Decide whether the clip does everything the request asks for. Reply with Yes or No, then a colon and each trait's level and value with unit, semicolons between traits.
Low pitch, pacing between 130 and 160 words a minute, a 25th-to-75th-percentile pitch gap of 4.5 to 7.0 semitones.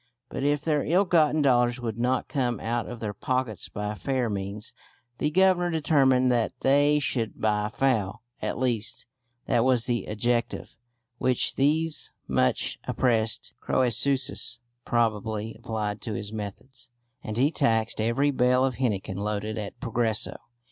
No: low, 120 Hz; average, 145 wpm; average, 3.8 semitones